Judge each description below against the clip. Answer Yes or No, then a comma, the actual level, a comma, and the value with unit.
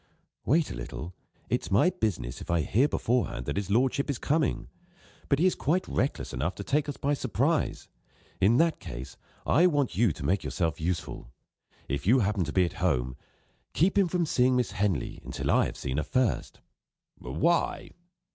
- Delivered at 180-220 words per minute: Yes, average, 185 wpm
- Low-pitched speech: Yes, low, 110 Hz